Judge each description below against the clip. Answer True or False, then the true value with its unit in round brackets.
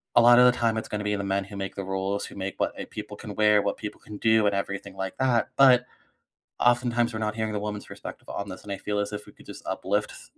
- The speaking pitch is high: False (105 Hz)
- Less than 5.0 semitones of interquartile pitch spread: True (2.4 semitones)